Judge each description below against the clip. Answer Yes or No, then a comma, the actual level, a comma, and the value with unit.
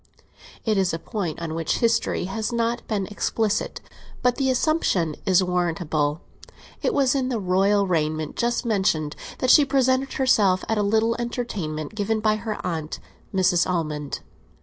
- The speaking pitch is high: Yes, high, 200 Hz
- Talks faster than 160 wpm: No, average, 155 wpm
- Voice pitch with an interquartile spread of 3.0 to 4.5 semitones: No, wide, 5.6 semitones